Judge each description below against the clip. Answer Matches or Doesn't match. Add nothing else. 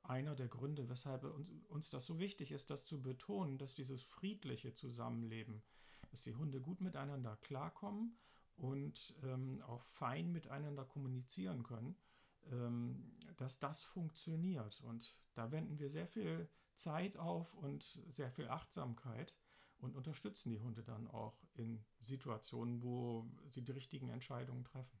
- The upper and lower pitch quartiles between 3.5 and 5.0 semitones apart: Matches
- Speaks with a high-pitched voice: Doesn't match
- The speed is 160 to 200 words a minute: Doesn't match